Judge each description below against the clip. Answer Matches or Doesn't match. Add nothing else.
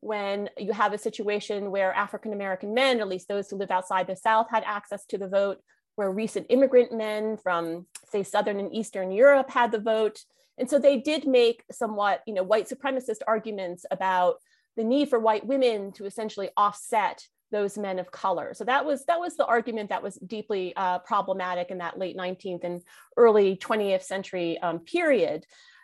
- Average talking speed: Matches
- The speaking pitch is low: Doesn't match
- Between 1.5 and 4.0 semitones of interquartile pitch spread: Matches